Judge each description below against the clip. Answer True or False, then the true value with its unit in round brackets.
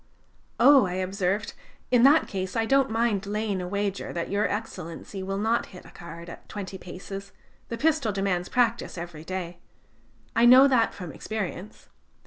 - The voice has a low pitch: False (200 Hz)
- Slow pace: False (165 wpm)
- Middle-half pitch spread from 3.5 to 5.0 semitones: True (3.8 semitones)